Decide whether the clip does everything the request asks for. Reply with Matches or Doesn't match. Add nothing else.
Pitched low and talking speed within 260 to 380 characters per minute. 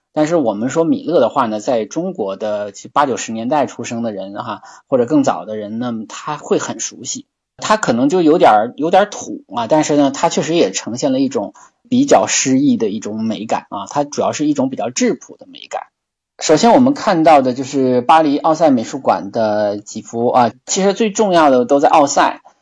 Doesn't match